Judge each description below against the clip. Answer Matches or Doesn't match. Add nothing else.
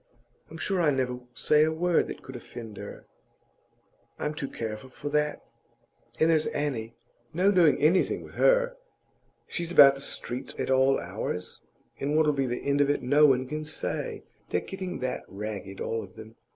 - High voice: Doesn't match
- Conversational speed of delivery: Matches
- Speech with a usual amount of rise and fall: Matches